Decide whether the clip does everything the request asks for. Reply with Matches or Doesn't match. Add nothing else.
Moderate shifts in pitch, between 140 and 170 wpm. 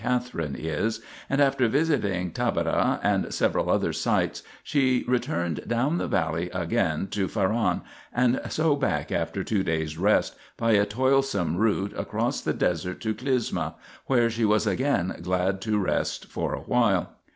Doesn't match